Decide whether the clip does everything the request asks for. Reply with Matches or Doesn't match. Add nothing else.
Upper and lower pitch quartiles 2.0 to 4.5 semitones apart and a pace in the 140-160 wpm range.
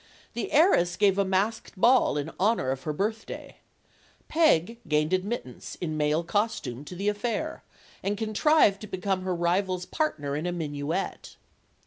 Doesn't match